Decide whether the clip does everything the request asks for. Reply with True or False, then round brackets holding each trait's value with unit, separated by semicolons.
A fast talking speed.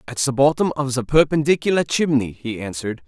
False (175 wpm)